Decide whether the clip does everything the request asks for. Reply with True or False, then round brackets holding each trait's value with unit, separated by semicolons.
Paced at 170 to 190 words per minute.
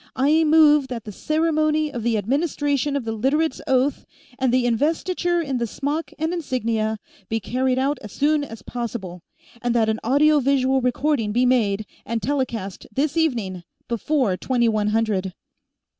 False (160 wpm)